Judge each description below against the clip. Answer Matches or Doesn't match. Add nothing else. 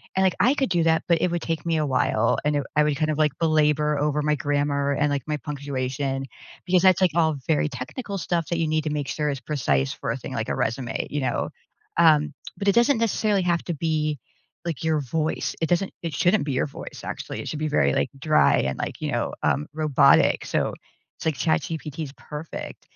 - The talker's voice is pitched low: Doesn't match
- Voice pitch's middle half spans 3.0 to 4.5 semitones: Doesn't match